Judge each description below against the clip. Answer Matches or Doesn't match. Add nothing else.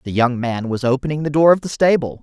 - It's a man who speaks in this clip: Matches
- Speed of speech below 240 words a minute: Doesn't match